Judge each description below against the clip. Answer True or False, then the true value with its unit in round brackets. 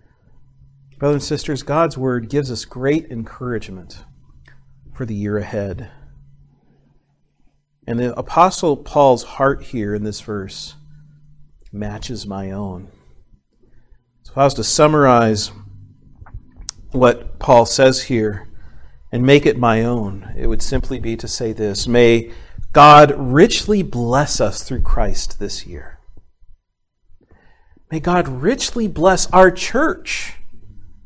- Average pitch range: False (5.8 semitones)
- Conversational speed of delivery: False (120 wpm)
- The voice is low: True (120 Hz)